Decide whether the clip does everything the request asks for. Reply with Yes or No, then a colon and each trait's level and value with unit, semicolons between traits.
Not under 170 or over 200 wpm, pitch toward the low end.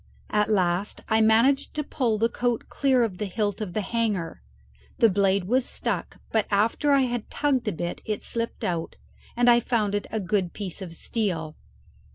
No: average, 190 wpm; high, 215 Hz